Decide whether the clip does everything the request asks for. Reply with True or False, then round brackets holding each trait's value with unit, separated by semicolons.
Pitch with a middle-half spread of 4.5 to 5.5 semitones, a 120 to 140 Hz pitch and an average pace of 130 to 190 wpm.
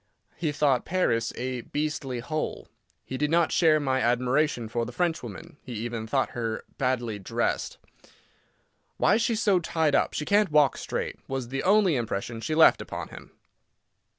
True (4.9 semitones; 135 Hz; 160 wpm)